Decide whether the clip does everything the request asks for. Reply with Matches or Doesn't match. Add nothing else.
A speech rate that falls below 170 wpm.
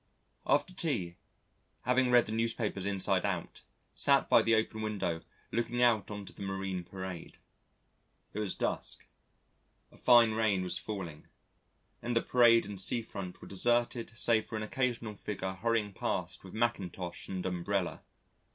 Matches